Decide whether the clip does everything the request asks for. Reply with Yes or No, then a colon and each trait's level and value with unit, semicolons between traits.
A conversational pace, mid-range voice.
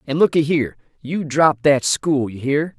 Yes: average, 195 wpm; medium, 145 Hz